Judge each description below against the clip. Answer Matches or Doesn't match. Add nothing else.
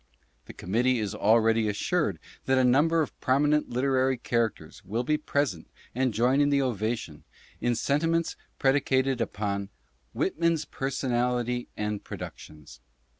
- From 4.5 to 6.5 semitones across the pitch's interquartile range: Doesn't match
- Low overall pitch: Matches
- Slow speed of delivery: Matches